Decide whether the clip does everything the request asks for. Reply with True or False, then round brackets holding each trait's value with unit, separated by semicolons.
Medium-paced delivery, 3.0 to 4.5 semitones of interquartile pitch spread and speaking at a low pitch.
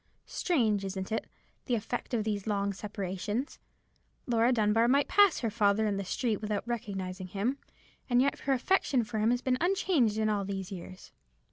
False (175 wpm; 3.5 semitones; 220 Hz)